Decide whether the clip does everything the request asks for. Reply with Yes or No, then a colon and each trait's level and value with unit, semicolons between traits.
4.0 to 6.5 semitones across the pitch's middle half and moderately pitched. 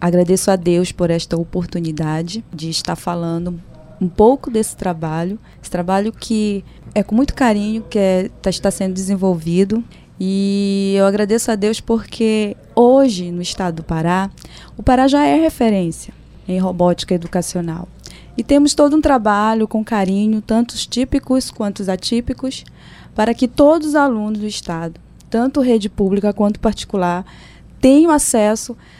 No: average, 4.3 semitones; high, 205 Hz